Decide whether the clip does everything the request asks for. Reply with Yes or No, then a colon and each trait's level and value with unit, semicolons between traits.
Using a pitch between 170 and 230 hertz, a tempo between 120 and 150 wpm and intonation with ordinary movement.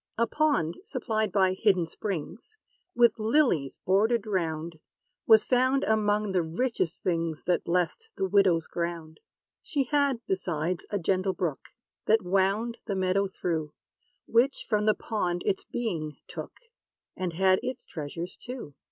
Yes: high, 190 Hz; average, 140 wpm; average, 4.9 semitones